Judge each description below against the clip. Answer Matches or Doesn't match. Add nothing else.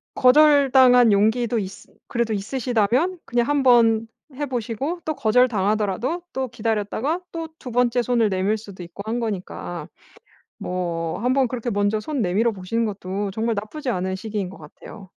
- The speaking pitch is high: Matches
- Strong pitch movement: Doesn't match